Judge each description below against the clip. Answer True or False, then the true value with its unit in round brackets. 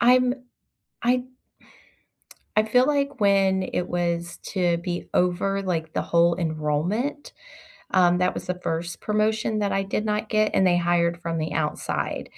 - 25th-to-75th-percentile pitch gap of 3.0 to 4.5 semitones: True (3.8 semitones)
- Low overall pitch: False (185 Hz)